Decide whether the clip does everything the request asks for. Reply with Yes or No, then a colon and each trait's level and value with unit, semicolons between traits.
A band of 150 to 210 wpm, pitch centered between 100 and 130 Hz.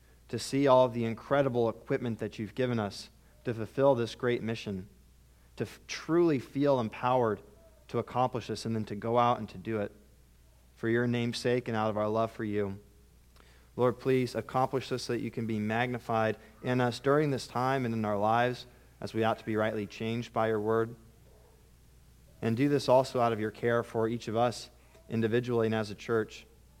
Yes: average, 200 wpm; low, 115 Hz